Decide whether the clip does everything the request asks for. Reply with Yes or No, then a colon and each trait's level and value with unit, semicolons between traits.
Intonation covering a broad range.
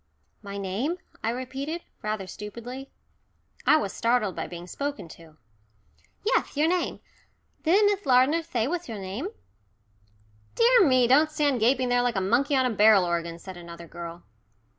Yes: wide, 7.1 semitones